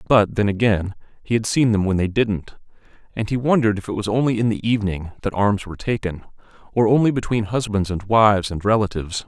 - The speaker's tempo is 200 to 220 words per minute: Yes, fast, 205 wpm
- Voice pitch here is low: Yes, low, 105 Hz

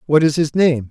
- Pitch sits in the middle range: Yes, medium, 150 Hz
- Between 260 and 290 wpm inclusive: Yes, fast, 265 wpm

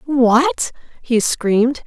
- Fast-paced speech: No, slow, 95 wpm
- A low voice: No, high, 235 Hz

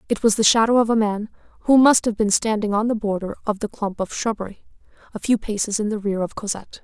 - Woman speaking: Yes, female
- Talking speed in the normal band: No, fast, 245 wpm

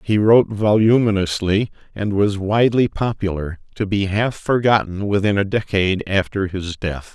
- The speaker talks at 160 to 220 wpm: No, average, 145 wpm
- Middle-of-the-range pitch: No, low, 100 Hz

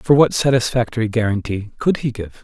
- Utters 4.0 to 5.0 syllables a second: No, 5.5 syllables/s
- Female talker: No, male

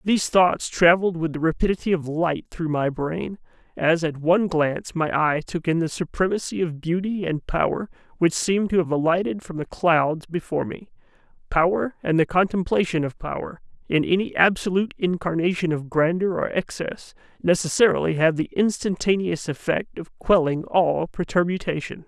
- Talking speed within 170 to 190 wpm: No, average, 160 wpm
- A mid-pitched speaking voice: Yes, medium, 170 Hz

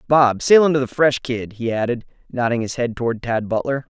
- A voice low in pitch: Yes, low, 125 Hz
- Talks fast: Yes, fast, 215 wpm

